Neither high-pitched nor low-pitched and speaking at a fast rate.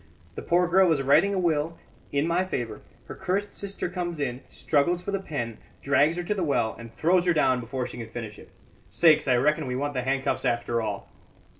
Yes: medium, 150 Hz; fast, 215 wpm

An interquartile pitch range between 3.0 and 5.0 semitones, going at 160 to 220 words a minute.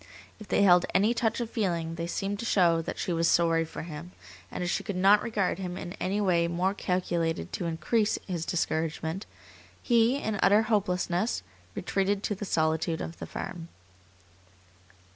Yes: average, 3.5 semitones; average, 175 wpm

